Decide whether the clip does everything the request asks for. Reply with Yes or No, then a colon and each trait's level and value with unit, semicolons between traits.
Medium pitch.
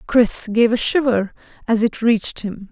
No: high, 225 Hz